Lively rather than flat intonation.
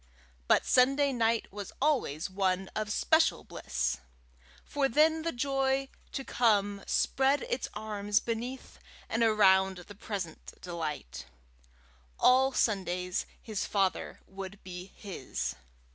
Yes: wide, 5.7 semitones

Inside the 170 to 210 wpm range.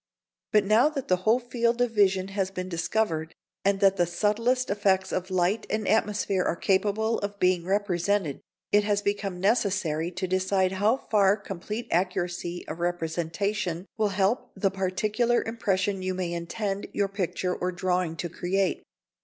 No: average, 160 wpm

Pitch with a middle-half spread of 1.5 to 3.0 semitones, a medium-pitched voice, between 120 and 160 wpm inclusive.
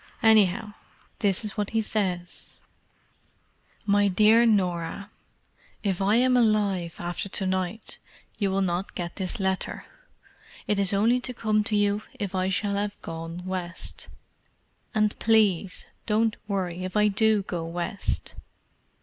No: narrow, 2.5 semitones; high, 200 Hz; average, 140 wpm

